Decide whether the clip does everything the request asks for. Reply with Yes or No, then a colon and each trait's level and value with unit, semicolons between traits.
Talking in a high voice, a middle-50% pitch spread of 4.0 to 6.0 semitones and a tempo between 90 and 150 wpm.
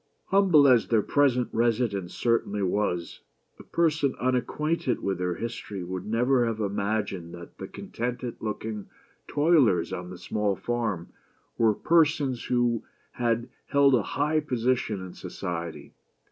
No: low, 115 Hz; average, 4.6 semitones; slow, 135 wpm